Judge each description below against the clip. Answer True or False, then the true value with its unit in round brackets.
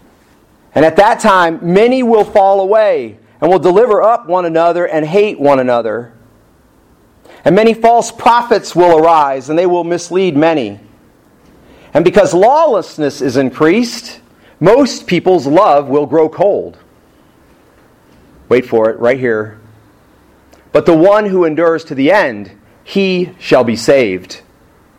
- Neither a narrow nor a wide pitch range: False (7.4 semitones)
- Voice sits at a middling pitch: True (165 Hz)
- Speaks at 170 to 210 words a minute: False (135 wpm)